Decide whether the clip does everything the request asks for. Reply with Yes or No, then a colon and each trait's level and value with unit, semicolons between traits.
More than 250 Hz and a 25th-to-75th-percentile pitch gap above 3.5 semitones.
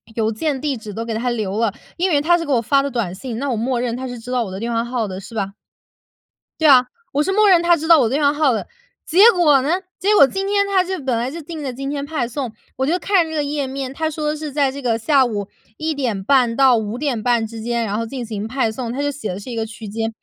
Yes: very high, 260 Hz; average, 4.7 semitones